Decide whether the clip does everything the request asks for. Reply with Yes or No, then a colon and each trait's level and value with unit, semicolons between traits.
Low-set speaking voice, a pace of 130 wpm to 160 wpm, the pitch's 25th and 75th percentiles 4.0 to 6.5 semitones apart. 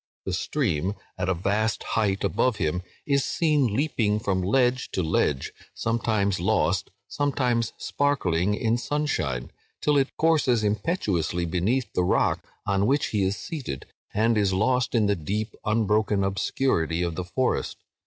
Yes: low, 105 Hz; average, 145 wpm; wide, 5.4 semitones